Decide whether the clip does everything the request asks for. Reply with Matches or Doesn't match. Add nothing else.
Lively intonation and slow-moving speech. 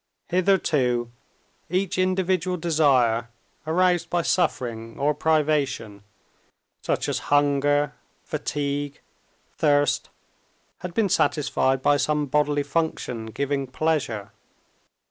Doesn't match